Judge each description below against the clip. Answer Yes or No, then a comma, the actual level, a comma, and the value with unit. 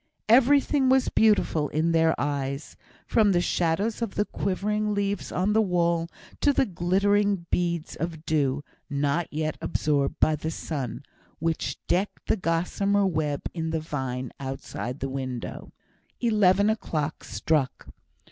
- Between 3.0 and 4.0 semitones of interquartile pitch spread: No, wide, 5.4 semitones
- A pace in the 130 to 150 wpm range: Yes, average, 140 wpm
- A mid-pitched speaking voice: Yes, medium, 170 Hz